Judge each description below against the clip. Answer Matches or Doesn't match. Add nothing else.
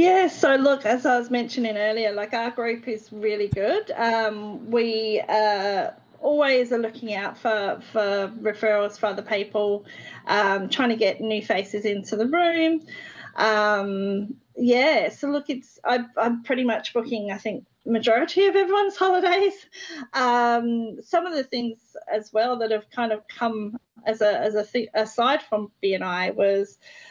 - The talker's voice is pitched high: Matches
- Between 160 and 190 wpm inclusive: Matches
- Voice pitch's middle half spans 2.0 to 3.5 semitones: Matches